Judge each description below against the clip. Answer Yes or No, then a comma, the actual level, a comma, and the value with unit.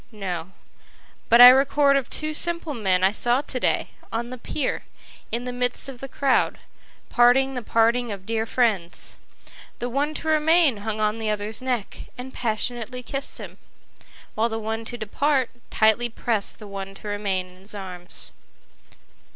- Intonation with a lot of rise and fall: No, average, 3.7 semitones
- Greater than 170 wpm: No, average, 160 wpm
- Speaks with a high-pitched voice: Yes, high, 235 Hz